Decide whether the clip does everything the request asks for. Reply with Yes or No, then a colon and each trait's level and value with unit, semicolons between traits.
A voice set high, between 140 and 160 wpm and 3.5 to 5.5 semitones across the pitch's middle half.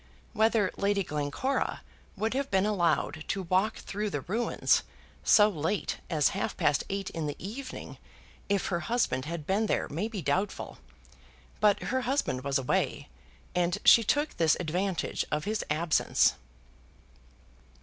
Yes: high, 195 Hz; average, 145 wpm; average, 5.2 semitones